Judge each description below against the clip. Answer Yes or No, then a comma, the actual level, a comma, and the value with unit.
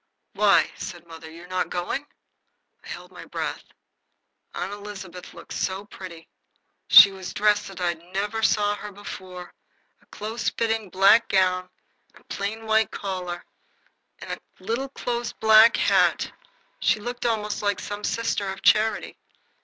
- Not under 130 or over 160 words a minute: Yes, average, 145 wpm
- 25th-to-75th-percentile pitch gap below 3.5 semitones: Yes, average, 3.1 semitones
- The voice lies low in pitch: No, high, 205 Hz